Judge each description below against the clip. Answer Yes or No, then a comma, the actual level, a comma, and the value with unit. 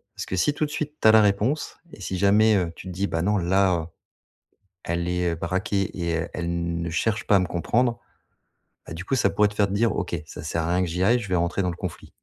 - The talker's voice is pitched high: No, very low, 95 Hz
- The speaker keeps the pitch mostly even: No, average, 3.4 semitones